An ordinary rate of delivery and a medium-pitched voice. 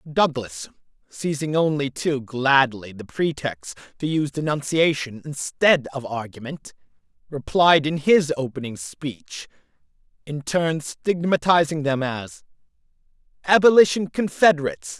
No: slow, 100 wpm; medium, 150 Hz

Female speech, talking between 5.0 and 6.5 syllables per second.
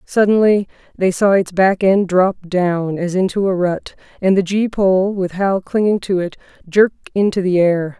No: female; 4.4 syllables/s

